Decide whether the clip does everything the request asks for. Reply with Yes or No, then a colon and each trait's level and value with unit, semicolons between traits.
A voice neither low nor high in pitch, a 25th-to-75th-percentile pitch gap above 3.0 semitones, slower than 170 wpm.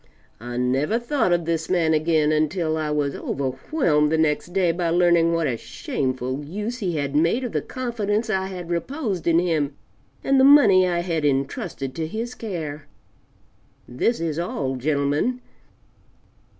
Yes: medium, 165 Hz; average, 4.5 semitones; average, 160 wpm